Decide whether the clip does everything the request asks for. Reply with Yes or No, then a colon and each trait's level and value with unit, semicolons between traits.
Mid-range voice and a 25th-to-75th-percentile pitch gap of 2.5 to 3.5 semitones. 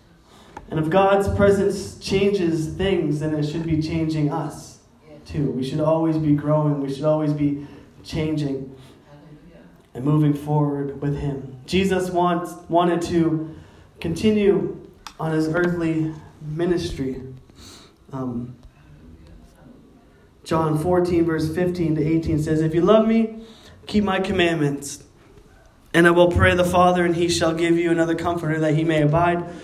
Yes: medium, 160 Hz; average, 3.0 semitones